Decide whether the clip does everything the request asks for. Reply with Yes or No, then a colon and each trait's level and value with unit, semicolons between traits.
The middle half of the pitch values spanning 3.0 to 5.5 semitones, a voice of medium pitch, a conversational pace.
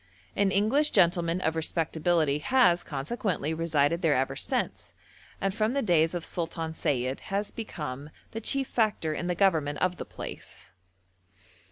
Yes: average, 4.3 semitones; medium, 170 Hz; average, 150 wpm